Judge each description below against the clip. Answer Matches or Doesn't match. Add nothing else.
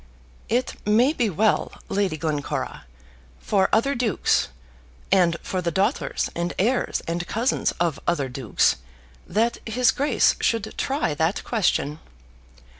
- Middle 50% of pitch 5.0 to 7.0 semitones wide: Matches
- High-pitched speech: Matches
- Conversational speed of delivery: Doesn't match